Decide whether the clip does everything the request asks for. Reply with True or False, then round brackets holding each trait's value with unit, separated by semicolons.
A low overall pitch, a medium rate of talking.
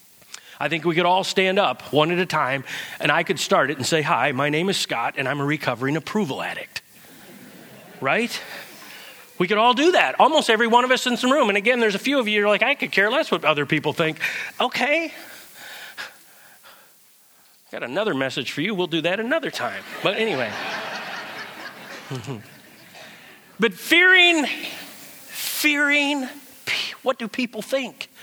False (215 Hz; 170 wpm)